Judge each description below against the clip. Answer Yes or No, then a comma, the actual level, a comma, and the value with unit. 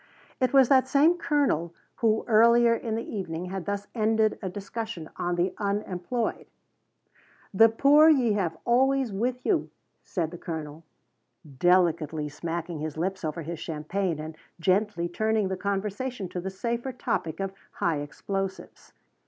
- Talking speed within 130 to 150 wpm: Yes, average, 145 wpm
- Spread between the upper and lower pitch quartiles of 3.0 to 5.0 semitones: No, wide, 5.4 semitones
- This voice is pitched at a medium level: No, high, 195 Hz